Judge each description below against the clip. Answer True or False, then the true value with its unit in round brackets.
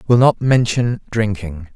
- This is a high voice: False (110 Hz)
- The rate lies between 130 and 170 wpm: True (135 wpm)